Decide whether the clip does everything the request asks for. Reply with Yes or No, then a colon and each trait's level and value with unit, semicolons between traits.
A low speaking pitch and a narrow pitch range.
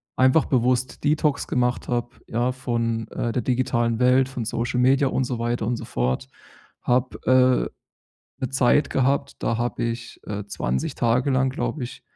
Yes: low, 125 Hz; narrow, 1.8 semitones